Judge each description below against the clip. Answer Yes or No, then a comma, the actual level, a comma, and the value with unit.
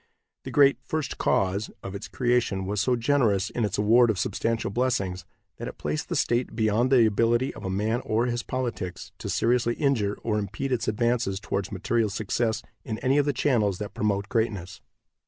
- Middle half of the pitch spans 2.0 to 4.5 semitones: Yes, average, 3.3 semitones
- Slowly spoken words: No, average, 185 wpm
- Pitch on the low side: Yes, low, 115 Hz